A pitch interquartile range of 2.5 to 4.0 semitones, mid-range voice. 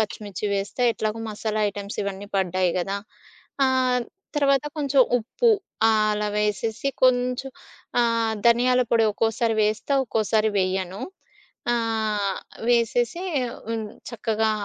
No: average, 2.8 semitones; high, 220 Hz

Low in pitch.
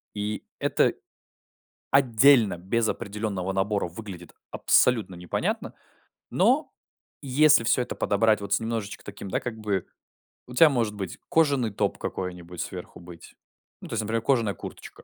Yes: low, 105 Hz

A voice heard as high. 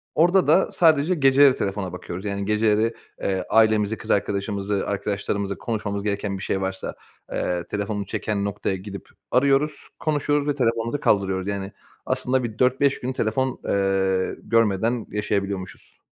No: low, 105 Hz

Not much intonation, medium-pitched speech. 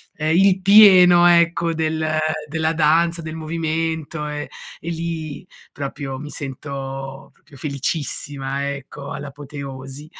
No: average, 3.0 semitones; medium, 155 Hz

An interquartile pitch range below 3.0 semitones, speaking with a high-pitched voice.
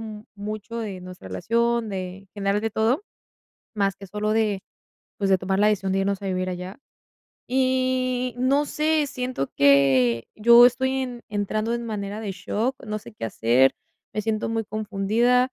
No: average, 3.6 semitones; high, 215 Hz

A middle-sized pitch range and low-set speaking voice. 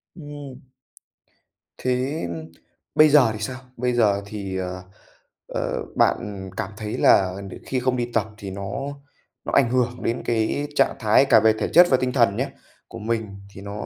Yes: average, 4.1 semitones; low, 115 Hz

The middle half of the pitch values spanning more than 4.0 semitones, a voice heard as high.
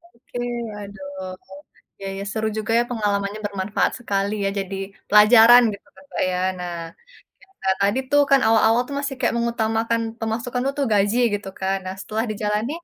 No: average, 2.9 semitones; high, 215 Hz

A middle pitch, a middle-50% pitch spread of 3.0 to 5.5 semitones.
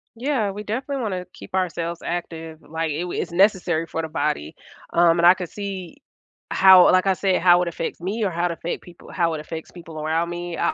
No: medium, 175 Hz; narrow, 2.4 semitones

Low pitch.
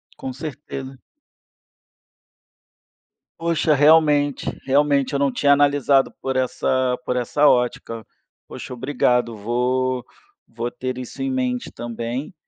Yes: low, 130 Hz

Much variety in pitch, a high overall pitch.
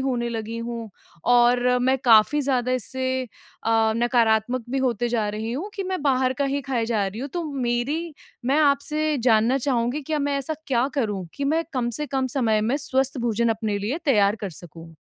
No: average, 3.4 semitones; high, 245 Hz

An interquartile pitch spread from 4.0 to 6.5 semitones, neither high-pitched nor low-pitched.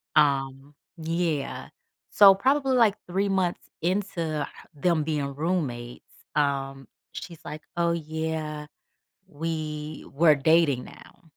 No: average, 3.0 semitones; medium, 160 Hz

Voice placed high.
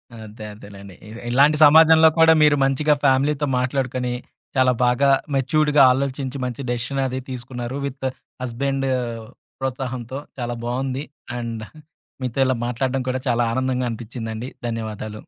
No: low, 130 Hz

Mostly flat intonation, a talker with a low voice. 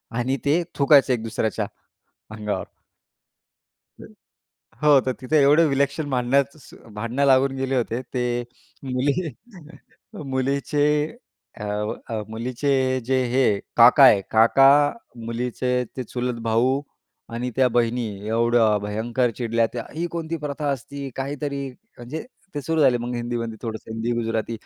No: average, 3.2 semitones; low, 125 Hz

